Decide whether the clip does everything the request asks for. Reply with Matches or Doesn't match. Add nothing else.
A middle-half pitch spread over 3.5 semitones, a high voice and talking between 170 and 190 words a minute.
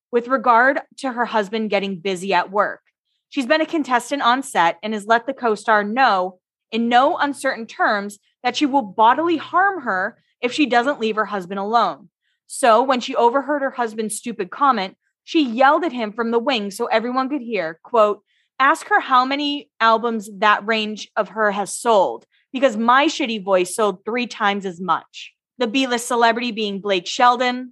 Matches